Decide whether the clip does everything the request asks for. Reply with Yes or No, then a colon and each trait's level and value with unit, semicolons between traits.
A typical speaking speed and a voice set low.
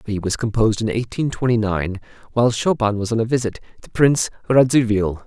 Yes: average, 180 wpm; low, 115 Hz